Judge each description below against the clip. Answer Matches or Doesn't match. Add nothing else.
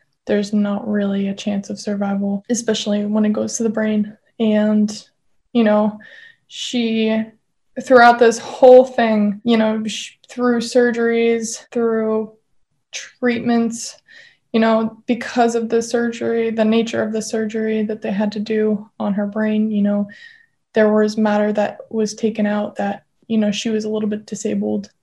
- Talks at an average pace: Matches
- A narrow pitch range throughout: Matches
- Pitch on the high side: Matches